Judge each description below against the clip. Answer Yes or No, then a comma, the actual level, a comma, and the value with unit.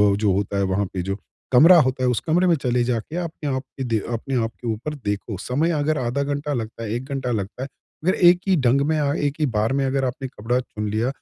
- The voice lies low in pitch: Yes, low, 130 Hz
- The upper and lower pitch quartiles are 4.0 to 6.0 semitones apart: Yes, average, 4.4 semitones